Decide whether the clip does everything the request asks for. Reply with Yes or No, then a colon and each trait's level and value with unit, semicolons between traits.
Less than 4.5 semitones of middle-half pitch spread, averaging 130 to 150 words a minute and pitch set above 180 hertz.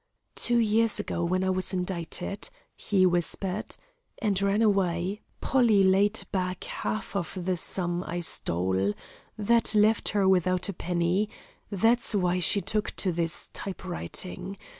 Yes: average, 2.8 semitones; average, 140 wpm; high, 190 Hz